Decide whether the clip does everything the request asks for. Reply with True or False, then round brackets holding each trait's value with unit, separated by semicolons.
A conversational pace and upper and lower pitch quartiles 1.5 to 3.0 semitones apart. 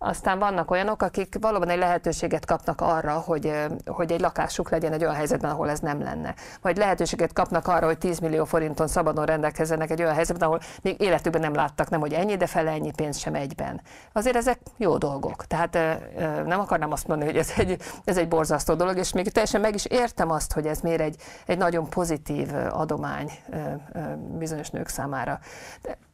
False (190 wpm; 2.4 semitones)